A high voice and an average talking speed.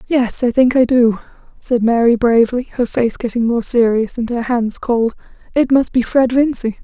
Yes: high, 240 Hz; average, 195 wpm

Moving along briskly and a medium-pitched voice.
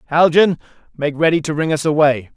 No: average, 180 wpm; medium, 155 Hz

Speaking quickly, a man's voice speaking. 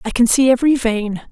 No: fast, 230 wpm; female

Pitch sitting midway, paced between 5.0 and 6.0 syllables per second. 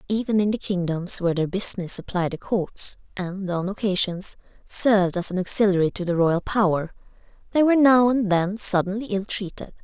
No: high, 195 Hz; 5.4 syllables/s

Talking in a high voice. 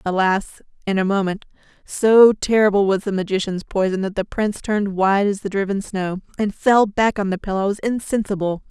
Yes: high, 200 Hz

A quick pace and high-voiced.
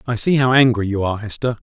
No: fast, 250 wpm; low, 115 Hz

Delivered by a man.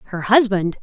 No: female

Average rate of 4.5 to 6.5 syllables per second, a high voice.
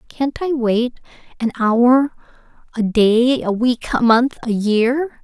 No: 3.4 syllables/s; high, 240 Hz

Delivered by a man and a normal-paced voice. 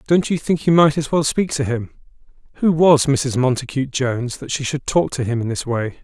No: male; fast, 240 wpm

